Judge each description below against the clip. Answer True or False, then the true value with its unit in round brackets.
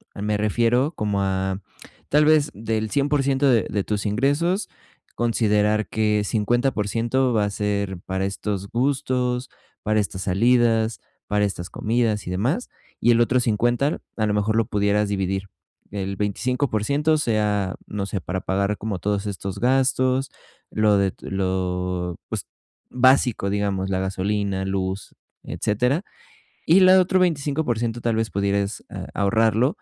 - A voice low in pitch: True (105 Hz)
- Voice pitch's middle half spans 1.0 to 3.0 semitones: False (4.0 semitones)